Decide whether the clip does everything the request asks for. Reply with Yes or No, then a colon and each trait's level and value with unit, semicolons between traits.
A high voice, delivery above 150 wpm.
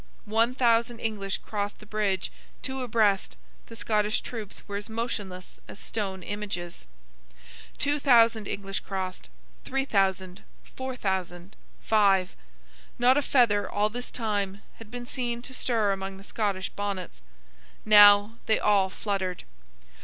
No: high, 210 Hz; slow, 135 wpm